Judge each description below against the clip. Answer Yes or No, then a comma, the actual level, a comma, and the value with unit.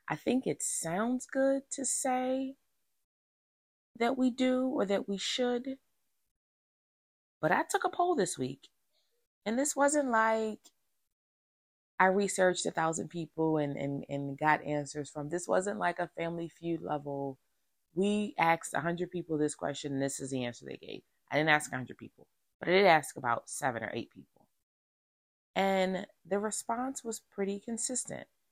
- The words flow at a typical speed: Yes, average, 165 wpm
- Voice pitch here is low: No, high, 190 Hz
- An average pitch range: No, wide, 8.6 semitones